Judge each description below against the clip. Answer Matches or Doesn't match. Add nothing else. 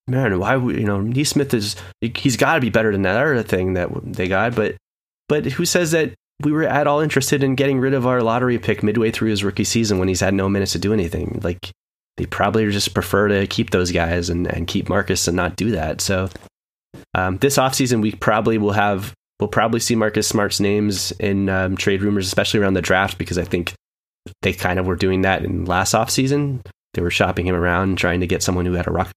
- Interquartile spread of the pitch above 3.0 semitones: Matches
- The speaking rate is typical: Doesn't match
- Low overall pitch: Matches